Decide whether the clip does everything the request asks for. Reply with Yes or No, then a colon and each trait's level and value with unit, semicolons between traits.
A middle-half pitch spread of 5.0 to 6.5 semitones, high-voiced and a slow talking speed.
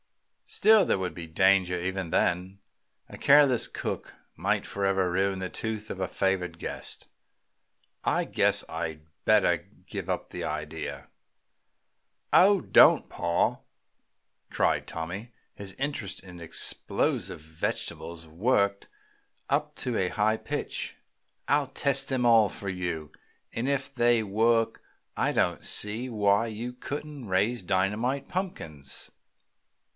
No: average, 5.3 semitones; low, 100 Hz; slow, 125 wpm